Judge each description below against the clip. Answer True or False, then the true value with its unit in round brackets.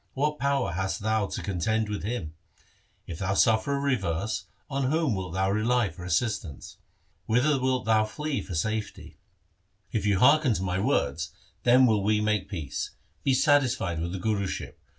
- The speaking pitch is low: True (110 Hz)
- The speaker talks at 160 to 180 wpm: True (170 wpm)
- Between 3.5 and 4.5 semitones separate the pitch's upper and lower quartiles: False (5.2 semitones)